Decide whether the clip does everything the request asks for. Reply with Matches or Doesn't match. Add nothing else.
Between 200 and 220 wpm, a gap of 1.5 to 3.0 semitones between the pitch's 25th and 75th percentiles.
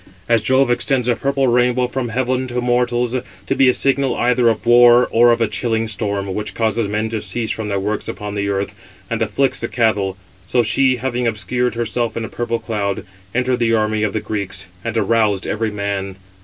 Matches